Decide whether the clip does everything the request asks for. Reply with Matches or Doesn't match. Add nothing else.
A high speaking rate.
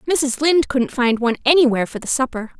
Matches